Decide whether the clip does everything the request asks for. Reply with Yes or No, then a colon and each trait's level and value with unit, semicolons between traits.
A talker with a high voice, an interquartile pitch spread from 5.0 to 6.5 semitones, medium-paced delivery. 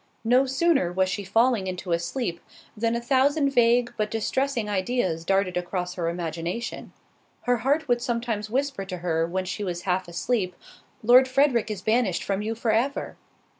Yes: high, 215 Hz; average, 5.3 semitones; average, 170 wpm